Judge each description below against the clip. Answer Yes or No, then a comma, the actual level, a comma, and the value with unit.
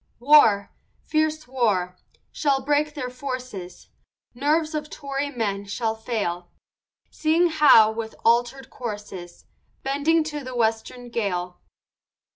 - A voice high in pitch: Yes, very high, 250 Hz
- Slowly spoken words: Yes, slow, 110 wpm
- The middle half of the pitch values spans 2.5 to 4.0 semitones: No, average, 5.1 semitones